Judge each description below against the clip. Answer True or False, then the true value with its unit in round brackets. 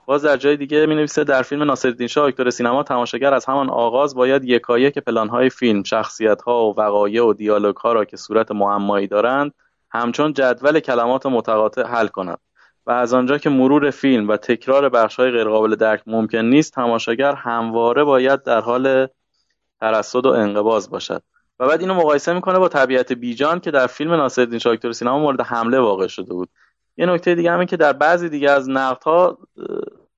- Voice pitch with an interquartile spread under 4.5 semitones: True (4.0 semitones)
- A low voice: True (130 Hz)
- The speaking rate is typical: False (180 wpm)